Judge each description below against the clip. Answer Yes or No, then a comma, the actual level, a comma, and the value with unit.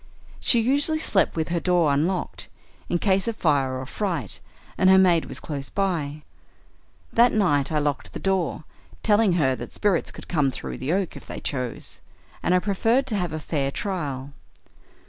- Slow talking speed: No, average, 180 wpm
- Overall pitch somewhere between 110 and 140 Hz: No, medium, 175 Hz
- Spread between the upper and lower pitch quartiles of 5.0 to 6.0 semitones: Yes, wide, 5.5 semitones